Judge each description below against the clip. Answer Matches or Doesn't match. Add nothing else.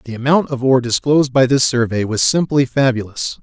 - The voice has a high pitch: Doesn't match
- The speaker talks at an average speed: Matches